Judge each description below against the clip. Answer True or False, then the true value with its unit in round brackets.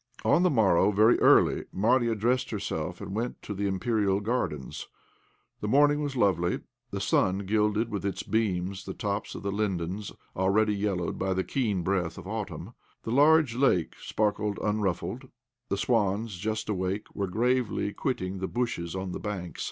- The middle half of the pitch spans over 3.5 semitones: False (3.2 semitones)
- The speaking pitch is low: True (105 Hz)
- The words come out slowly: False (165 wpm)